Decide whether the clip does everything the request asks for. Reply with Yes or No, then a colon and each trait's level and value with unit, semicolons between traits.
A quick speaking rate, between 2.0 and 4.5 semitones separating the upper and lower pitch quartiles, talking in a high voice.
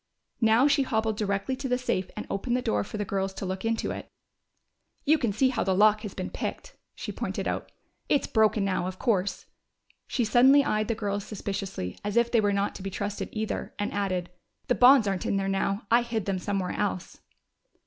Yes: fast, 210 wpm; average, 3.3 semitones; high, 210 Hz